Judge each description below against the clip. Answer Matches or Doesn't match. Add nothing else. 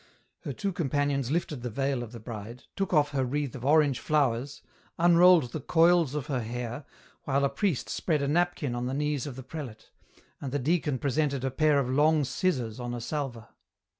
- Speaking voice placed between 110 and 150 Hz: Matches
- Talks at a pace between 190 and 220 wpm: Matches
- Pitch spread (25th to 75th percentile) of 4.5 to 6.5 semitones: Doesn't match